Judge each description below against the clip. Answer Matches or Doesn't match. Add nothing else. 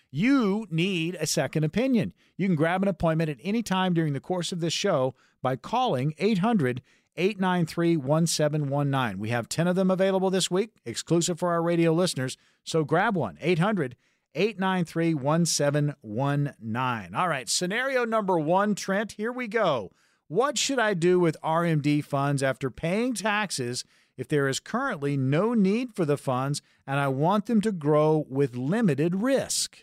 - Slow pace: Doesn't match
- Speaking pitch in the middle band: Matches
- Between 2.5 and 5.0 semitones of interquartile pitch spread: Doesn't match